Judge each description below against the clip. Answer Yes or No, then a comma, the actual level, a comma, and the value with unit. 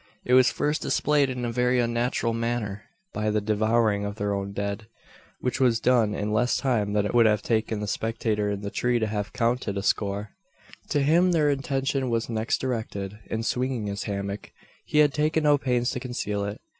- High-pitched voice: No, low, 115 Hz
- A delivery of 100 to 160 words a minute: No, average, 200 wpm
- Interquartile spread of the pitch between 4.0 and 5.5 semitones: No, average, 3.4 semitones